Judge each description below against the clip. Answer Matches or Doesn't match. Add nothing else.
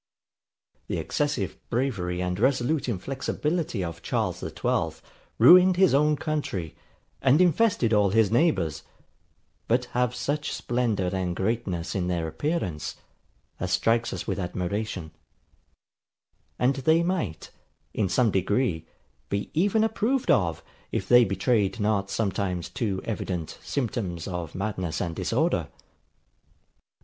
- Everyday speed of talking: Doesn't match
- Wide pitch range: Matches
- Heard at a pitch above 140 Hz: Doesn't match